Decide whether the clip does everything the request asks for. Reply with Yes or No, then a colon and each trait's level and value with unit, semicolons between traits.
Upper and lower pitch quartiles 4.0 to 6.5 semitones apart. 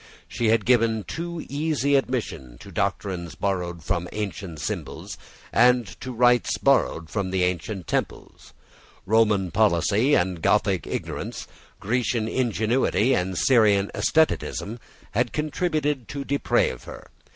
Yes: average, 5.3 semitones